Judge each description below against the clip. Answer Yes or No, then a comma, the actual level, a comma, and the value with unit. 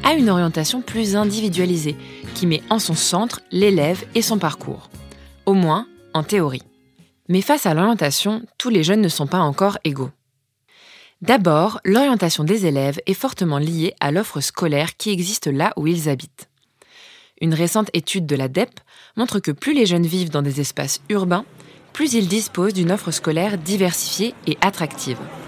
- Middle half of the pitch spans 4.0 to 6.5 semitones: Yes, wide, 5.5 semitones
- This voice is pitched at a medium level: Yes, medium, 180 Hz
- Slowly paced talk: No, average, 165 wpm